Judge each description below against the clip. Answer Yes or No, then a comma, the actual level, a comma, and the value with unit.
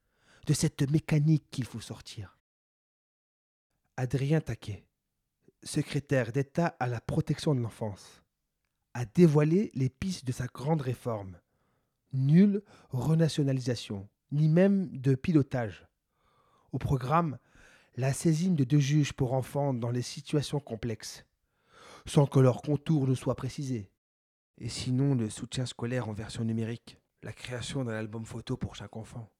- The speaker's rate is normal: No, slow, 135 wpm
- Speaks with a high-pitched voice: No, low, 130 Hz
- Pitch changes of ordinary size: Yes, average, 4.5 semitones